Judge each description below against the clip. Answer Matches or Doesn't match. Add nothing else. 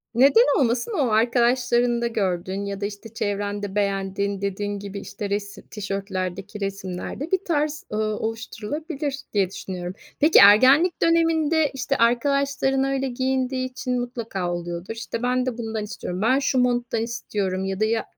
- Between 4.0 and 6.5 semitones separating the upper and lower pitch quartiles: Matches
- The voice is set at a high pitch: Matches